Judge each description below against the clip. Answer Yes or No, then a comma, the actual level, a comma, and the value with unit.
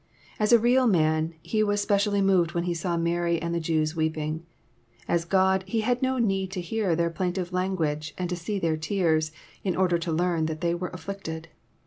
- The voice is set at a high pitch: No, medium, 175 Hz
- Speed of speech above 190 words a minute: Yes, average, 200 wpm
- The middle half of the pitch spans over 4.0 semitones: No, average, 3.1 semitones